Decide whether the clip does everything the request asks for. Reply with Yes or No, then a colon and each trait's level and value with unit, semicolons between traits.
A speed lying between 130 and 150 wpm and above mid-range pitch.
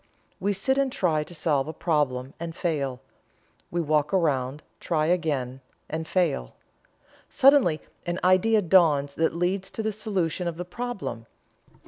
No: average, 145 wpm; medium, 165 Hz